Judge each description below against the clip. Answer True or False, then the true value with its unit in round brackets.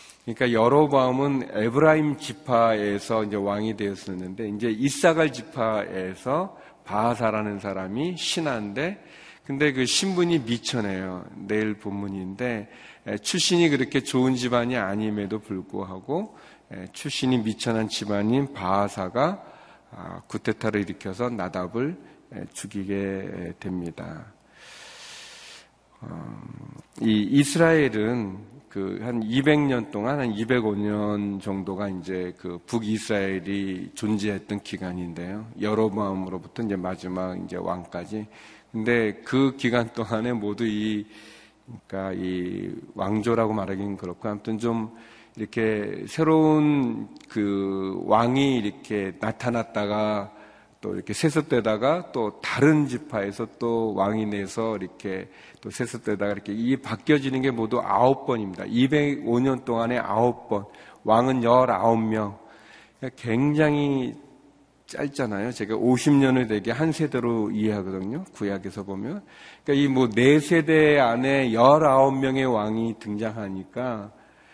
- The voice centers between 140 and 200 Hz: False (110 Hz)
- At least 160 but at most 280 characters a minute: True (260 characters per minute)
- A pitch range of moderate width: True (4.0 semitones)